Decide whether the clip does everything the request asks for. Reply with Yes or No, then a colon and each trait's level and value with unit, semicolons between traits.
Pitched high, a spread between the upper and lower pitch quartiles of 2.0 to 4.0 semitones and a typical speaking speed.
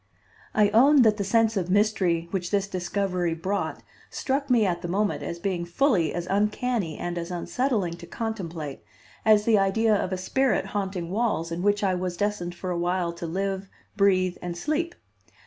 Yes: high, 195 Hz; average, 3.5 semitones; average, 180 wpm